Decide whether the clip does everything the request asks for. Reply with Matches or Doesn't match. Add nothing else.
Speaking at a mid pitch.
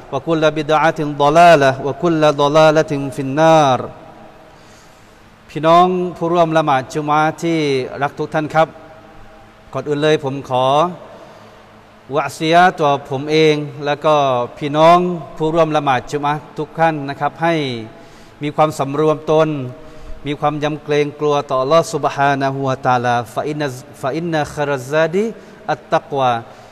Matches